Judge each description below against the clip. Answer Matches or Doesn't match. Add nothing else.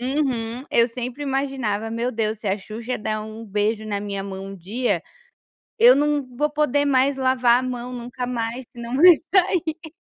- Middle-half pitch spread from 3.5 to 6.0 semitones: Matches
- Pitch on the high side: Matches